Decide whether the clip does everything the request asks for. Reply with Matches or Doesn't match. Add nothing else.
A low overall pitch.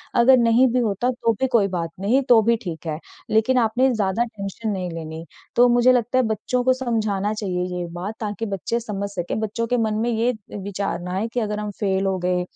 Doesn't match